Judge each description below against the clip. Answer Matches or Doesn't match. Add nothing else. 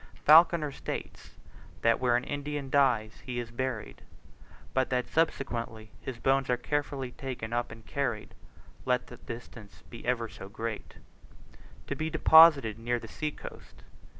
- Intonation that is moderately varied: Matches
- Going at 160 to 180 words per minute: Doesn't match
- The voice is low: Matches